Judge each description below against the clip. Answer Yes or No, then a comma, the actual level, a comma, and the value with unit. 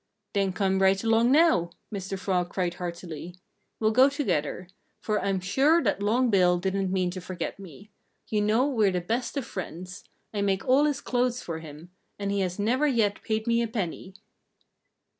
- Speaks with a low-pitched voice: No, high, 200 Hz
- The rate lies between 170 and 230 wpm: Yes, average, 180 wpm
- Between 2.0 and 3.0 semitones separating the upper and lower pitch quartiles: No, average, 4.2 semitones